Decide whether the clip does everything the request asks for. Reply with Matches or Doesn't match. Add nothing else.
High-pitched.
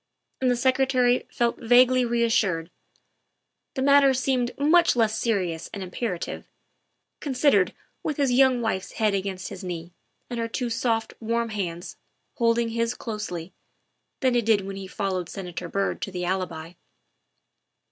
Matches